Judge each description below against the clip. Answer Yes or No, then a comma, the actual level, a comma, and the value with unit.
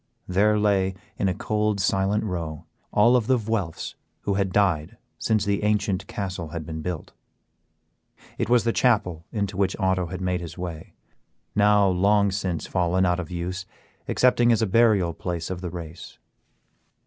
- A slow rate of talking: No, average, 165 wpm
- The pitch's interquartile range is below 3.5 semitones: Yes, average, 2.9 semitones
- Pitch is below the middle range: Yes, very low, 95 Hz